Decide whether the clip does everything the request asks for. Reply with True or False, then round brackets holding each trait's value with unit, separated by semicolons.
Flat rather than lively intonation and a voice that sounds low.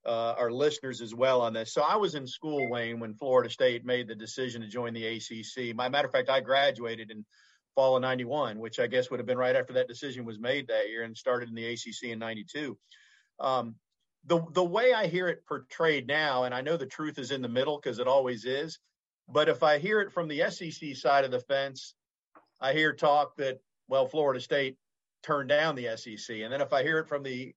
False (4.0 semitones; 130 Hz)